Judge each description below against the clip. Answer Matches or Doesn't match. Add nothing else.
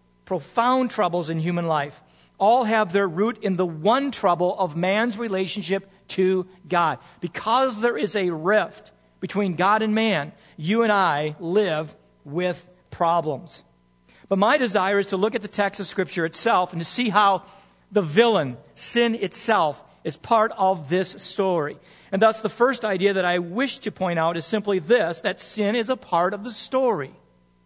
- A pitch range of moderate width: Matches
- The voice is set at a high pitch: Matches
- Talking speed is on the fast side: Doesn't match